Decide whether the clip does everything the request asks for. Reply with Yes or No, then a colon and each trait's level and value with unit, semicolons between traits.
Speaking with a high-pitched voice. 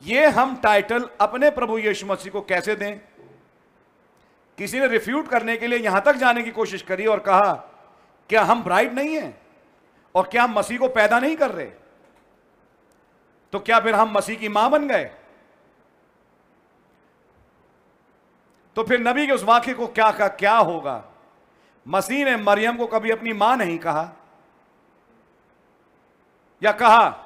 Yes: high, 225 Hz